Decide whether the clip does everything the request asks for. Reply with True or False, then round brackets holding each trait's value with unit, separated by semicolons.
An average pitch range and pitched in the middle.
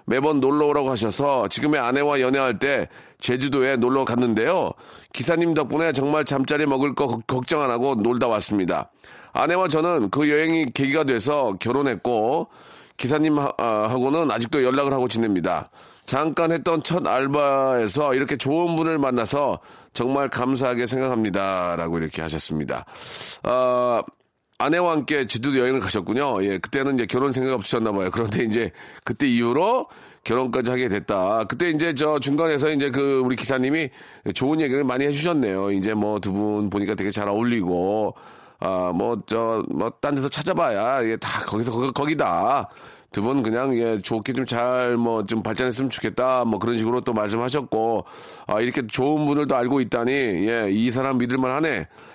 False (4.0 semitones; 130 Hz)